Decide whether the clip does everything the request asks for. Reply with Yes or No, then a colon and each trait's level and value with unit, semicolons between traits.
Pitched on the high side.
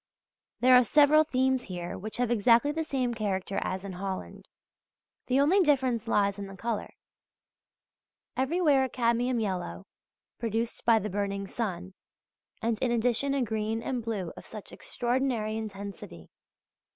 Yes: high, 230 Hz